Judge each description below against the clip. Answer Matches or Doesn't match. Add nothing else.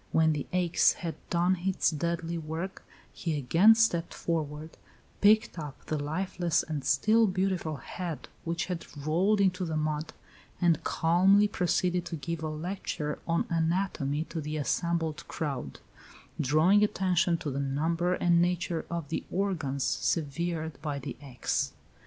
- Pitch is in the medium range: Matches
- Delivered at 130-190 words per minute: Matches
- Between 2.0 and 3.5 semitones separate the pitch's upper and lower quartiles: Matches